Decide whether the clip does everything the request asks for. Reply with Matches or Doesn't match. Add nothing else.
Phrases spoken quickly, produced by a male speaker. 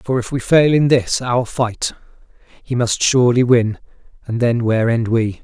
Doesn't match